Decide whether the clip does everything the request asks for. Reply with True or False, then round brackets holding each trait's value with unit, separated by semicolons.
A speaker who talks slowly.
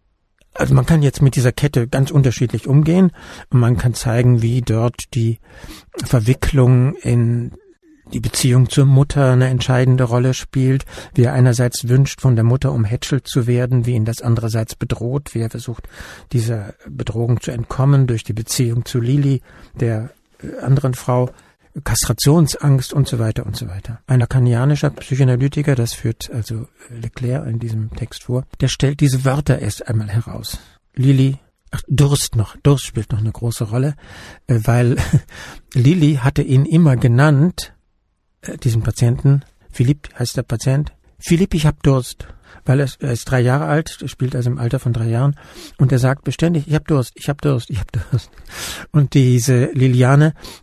False (160 wpm)